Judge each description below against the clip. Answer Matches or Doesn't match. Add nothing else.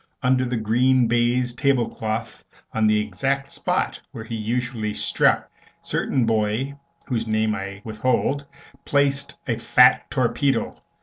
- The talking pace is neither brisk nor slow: Doesn't match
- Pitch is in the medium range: Doesn't match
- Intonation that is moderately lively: Matches